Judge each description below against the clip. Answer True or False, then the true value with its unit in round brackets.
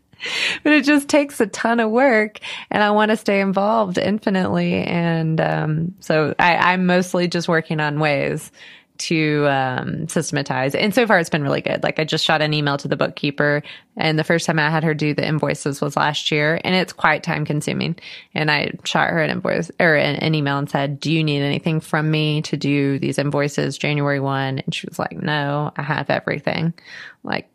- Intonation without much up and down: False (3.8 semitones)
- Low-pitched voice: False (160 Hz)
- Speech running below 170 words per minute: False (205 wpm)